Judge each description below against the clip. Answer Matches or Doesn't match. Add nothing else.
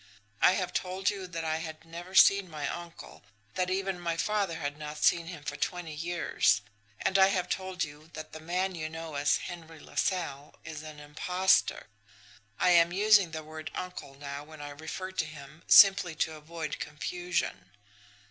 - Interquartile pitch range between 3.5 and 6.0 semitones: Doesn't match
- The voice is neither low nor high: Matches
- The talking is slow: Doesn't match